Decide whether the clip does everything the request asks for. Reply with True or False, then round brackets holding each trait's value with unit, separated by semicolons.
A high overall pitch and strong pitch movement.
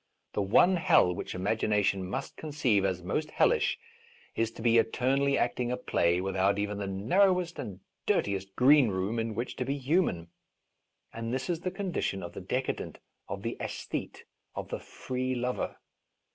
False (115 Hz; 6.1 semitones)